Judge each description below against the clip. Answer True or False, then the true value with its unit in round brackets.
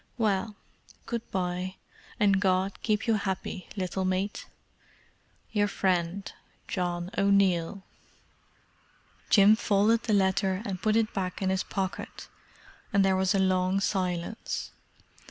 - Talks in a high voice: True (195 Hz)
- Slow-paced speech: True (120 wpm)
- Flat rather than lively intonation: True (1.8 semitones)